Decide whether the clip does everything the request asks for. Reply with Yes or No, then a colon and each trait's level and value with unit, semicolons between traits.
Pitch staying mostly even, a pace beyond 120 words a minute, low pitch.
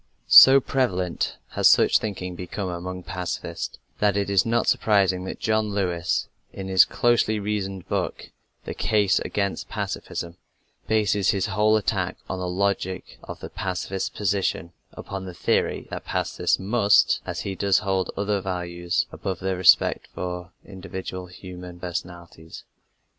Yes: narrow, 2.1 semitones; average, 140 wpm; very low, 95 Hz